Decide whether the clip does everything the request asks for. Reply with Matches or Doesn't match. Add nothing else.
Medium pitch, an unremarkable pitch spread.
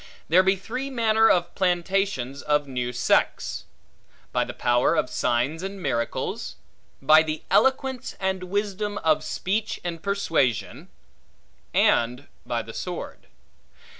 Doesn't match